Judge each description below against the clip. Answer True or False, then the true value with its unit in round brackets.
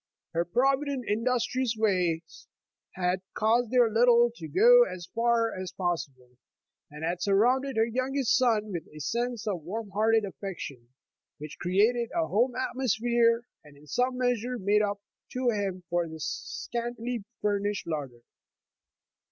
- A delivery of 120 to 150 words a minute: True (145 wpm)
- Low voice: False (220 Hz)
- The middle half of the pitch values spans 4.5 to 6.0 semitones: True (5.3 semitones)